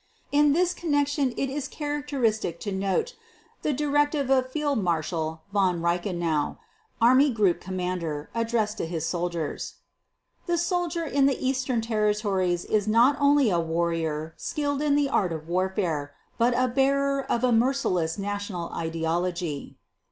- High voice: Yes, high, 215 Hz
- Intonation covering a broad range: Yes, wide, 8.2 semitones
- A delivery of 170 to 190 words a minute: No, slow, 135 wpm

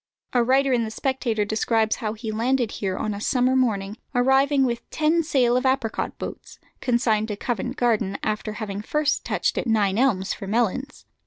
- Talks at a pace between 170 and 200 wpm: Yes, average, 180 wpm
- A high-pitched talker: Yes, high, 235 Hz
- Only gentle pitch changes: No, average, 3.5 semitones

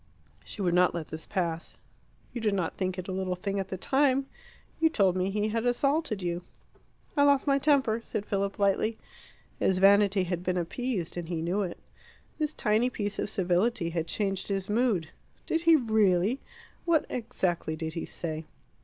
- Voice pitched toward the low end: No, high, 195 Hz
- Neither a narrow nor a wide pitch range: Yes, average, 4.9 semitones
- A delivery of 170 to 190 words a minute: Yes, average, 180 wpm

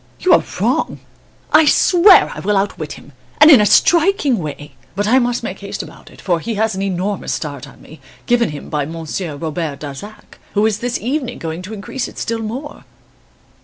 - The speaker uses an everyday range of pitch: No, wide, 6.9 semitones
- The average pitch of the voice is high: Yes, high, 205 Hz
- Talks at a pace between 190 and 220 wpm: Yes, average, 200 wpm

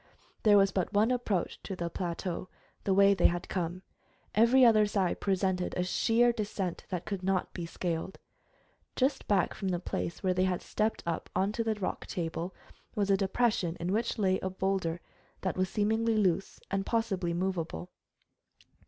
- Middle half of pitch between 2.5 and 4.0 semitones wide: Yes, average, 2.8 semitones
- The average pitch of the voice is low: No, high, 190 Hz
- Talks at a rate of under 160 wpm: No, average, 170 wpm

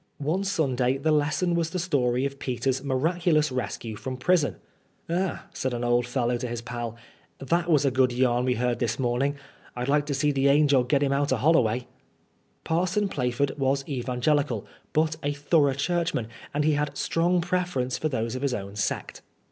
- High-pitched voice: No, medium, 140 Hz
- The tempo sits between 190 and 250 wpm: Yes, average, 195 wpm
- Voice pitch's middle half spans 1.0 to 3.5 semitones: No, average, 3.9 semitones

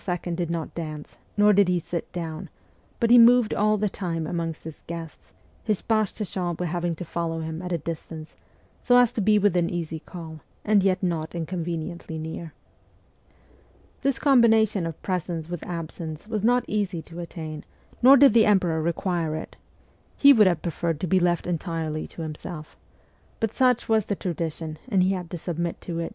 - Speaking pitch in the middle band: Yes, medium, 175 Hz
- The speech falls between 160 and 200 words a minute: Yes, average, 180 wpm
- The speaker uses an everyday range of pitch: Yes, average, 4.1 semitones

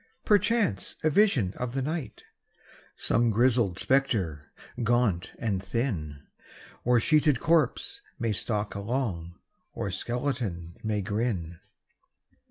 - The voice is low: Yes, low, 115 Hz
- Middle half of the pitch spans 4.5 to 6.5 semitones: Yes, wide, 5.6 semitones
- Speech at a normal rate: No, slow, 105 wpm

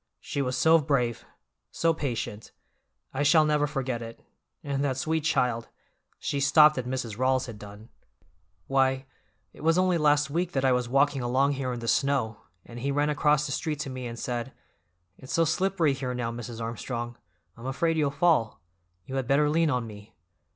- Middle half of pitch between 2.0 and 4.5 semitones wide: Yes, average, 3.6 semitones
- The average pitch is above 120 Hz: Yes, low, 135 Hz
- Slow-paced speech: No, average, 185 wpm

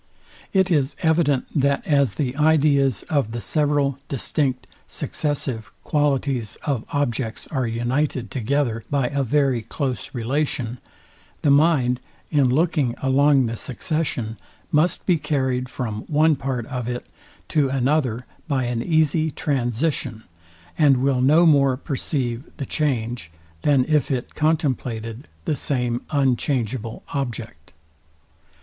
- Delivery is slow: Yes, slow, 125 wpm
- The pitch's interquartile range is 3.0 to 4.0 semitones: Yes, average, 3.3 semitones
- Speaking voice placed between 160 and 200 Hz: No, low, 135 Hz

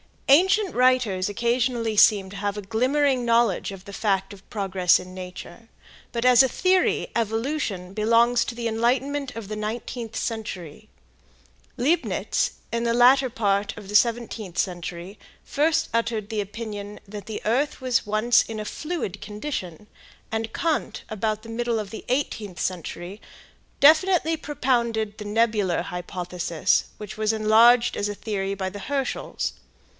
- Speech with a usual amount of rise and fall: Yes, average, 3.3 semitones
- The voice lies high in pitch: Yes, high, 220 Hz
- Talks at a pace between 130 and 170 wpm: Yes, average, 150 wpm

